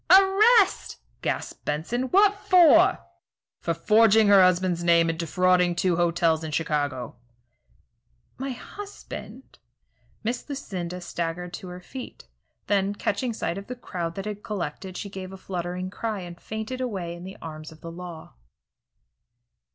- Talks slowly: No, average, 145 wpm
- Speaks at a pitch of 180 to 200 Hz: Yes, medium, 185 Hz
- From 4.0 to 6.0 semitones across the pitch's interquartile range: Yes, average, 4.8 semitones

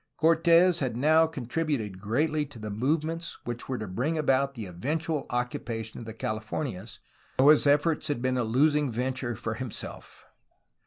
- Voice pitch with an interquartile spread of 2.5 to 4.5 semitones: No, average, 5.3 semitones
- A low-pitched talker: Yes, low, 130 Hz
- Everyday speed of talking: Yes, average, 160 wpm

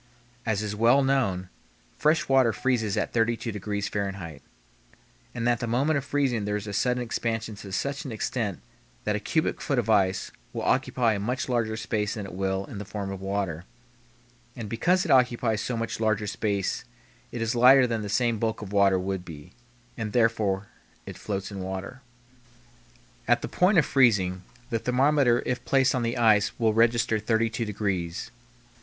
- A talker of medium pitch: No, low, 110 Hz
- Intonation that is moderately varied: Yes, average, 3.5 semitones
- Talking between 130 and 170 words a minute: No, average, 180 wpm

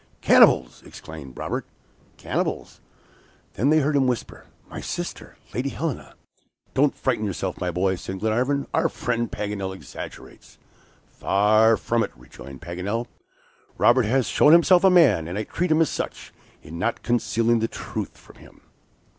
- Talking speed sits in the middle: Yes, average, 150 wpm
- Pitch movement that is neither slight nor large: No, wide, 6.0 semitones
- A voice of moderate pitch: No, low, 115 Hz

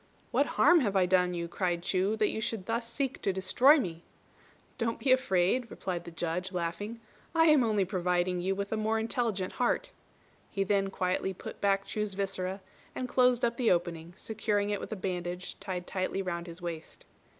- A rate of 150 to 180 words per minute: No, average, 190 wpm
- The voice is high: Yes, high, 195 Hz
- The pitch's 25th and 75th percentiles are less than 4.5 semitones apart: Yes, average, 3.7 semitones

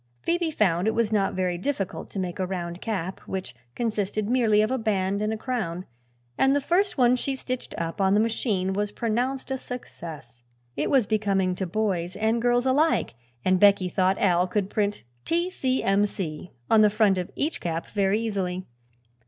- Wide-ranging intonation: No, average, 4.3 semitones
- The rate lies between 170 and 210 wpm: Yes, average, 190 wpm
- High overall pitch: Yes, high, 205 Hz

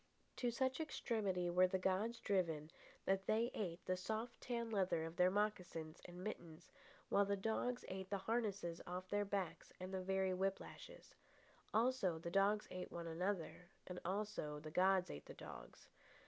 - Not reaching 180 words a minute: Yes, average, 170 wpm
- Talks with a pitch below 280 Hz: Yes, high, 190 Hz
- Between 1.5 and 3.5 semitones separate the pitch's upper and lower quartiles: Yes, average, 3.0 semitones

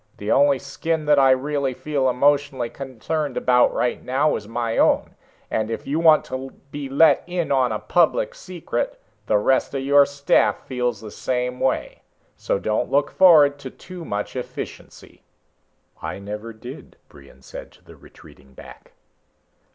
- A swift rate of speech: No, average, 160 wpm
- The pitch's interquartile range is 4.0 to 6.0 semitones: No, average, 3.2 semitones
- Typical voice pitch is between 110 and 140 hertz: Yes, low, 135 Hz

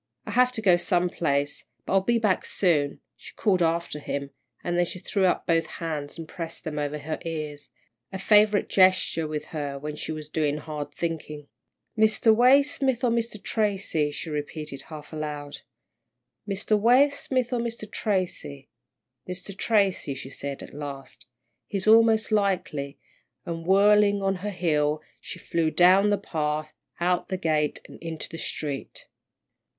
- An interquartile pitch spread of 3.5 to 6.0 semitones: Yes, average, 5.3 semitones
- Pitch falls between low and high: Yes, medium, 170 Hz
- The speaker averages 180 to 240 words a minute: No, average, 155 wpm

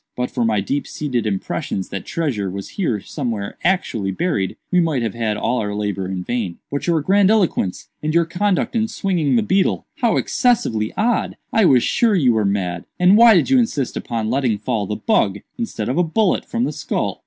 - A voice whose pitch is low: Yes, low, 130 Hz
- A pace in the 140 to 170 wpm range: No, average, 200 wpm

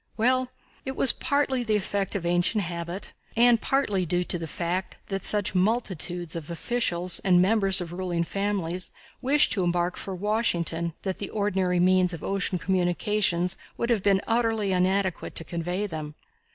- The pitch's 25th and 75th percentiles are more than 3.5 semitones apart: No, average, 3.2 semitones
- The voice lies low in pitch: No, medium, 185 Hz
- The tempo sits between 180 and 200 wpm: No, average, 165 wpm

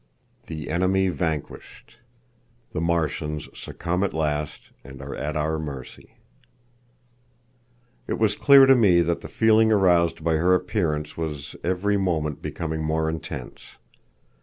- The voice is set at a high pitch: No, very low, 80 Hz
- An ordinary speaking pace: No, slow, 130 wpm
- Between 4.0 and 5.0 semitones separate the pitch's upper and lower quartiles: No, average, 3.5 semitones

